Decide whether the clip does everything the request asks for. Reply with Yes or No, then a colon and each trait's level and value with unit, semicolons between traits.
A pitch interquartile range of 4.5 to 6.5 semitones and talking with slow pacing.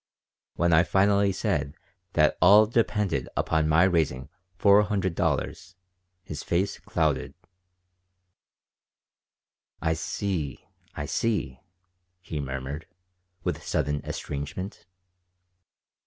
Yes: average, 5.1 semitones; slow, 95 wpm